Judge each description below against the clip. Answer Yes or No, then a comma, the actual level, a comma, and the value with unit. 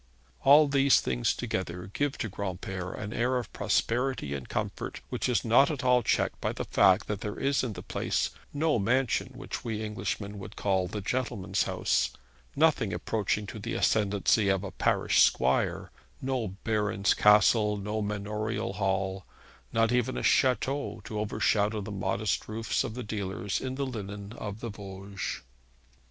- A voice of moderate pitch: No, low, 105 Hz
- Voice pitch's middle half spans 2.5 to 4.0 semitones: Yes, average, 3.6 semitones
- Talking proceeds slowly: No, average, 165 wpm